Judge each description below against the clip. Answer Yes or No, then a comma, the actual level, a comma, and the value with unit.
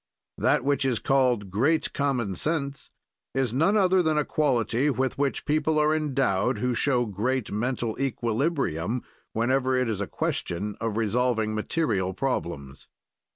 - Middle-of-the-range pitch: No, low, 125 Hz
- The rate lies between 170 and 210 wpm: No, average, 145 wpm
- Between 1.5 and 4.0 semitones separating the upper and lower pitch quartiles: No, average, 4.5 semitones